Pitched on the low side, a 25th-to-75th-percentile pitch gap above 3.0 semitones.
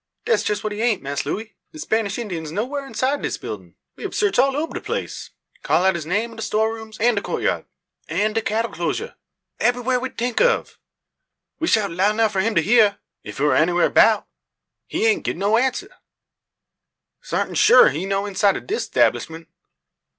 No: high, 220 Hz; average, 4.2 semitones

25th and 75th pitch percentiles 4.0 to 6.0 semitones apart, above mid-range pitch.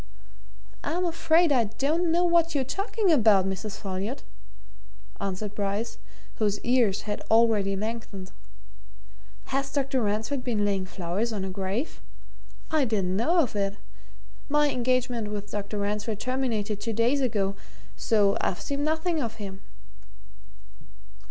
Yes: wide, 5.4 semitones; high, 225 Hz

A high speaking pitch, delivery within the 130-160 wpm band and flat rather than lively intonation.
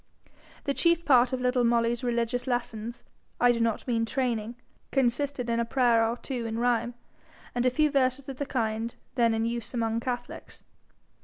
No: high, 240 Hz; average, 175 wpm; narrow, 1.8 semitones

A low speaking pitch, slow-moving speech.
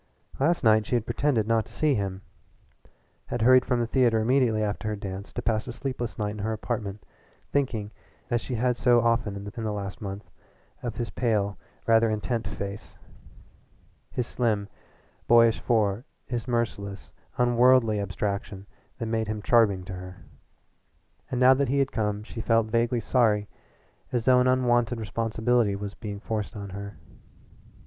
No: low, 110 Hz; average, 165 wpm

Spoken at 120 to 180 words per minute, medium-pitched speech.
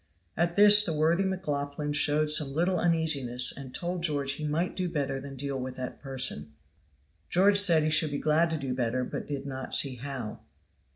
No: average, 190 wpm; medium, 150 Hz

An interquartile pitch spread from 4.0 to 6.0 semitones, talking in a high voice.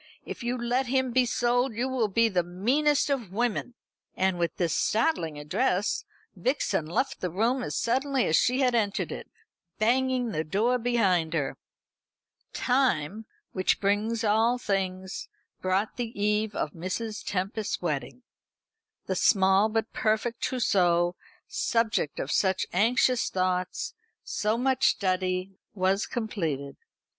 Yes: average, 4.8 semitones; high, 215 Hz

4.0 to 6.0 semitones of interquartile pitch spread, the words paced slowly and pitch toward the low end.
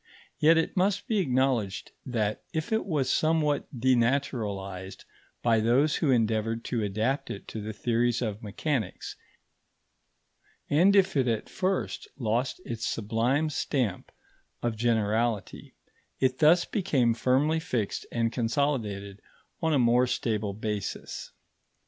Yes: average, 4.9 semitones; slow, 125 wpm; low, 120 Hz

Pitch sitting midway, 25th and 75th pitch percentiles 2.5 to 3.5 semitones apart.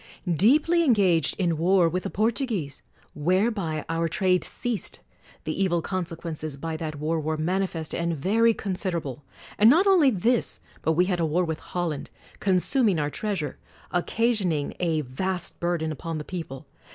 No: medium, 175 Hz; average, 4.0 semitones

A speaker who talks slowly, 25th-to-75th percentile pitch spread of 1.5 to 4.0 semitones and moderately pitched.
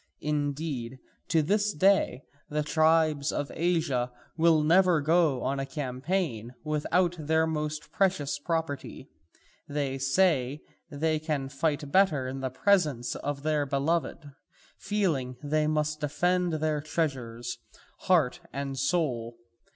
Yes: slow, 120 wpm; average, 3.1 semitones; medium, 150 Hz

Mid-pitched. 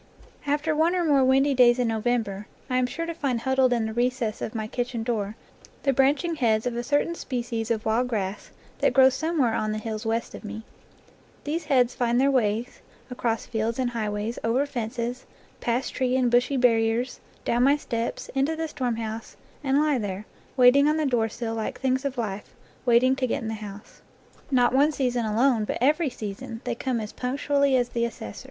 No: high, 245 Hz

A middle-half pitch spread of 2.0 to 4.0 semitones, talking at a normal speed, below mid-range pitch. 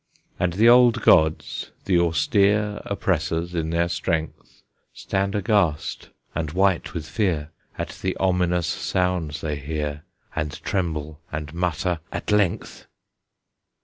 No: average, 3.6 semitones; slow, 120 wpm; very low, 85 Hz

